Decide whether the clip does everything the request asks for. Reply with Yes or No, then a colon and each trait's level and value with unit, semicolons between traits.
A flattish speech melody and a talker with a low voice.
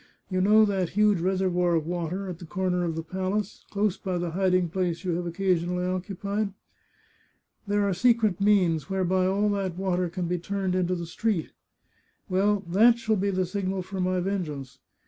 No: narrow, 2.2 semitones; medium, 185 Hz